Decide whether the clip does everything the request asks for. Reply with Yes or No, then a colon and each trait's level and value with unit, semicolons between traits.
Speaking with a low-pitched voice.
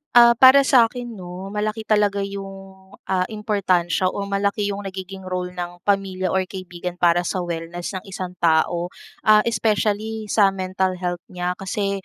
No: high, 195 Hz